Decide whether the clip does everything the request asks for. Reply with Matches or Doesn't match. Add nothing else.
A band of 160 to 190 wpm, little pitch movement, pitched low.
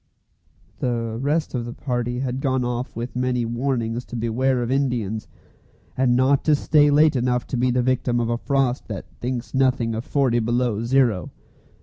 Matches